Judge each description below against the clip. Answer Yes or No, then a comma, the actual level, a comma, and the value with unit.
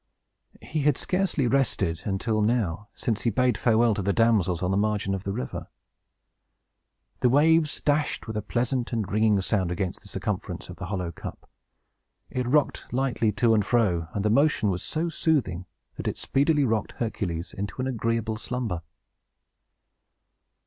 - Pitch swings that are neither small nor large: Yes, average, 4.6 semitones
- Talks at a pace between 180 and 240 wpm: No, average, 165 wpm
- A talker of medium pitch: No, low, 110 Hz